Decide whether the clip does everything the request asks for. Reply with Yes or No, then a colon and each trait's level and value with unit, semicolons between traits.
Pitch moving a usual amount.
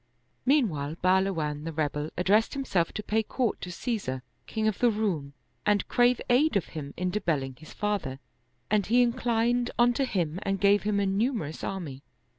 No: wide, 6.4 semitones